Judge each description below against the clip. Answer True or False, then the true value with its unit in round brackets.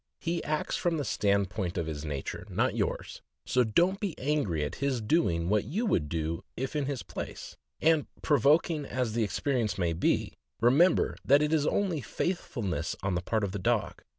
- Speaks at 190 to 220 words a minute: True (195 wpm)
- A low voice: True (125 Hz)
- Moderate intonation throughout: False (8.6 semitones)